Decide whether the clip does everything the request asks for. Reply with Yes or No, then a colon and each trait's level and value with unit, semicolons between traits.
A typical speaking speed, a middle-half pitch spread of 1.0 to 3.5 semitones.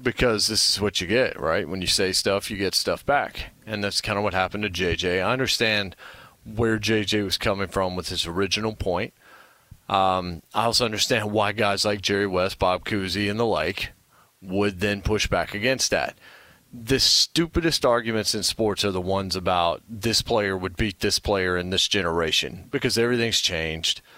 Yes: average, 185 wpm; average, 3.0 semitones